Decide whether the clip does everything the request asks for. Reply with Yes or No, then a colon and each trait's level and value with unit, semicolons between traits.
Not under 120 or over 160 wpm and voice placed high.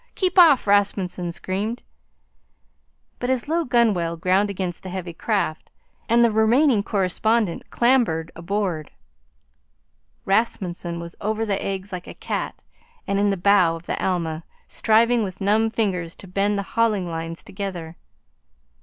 Yes: average, 140 wpm; high, 200 Hz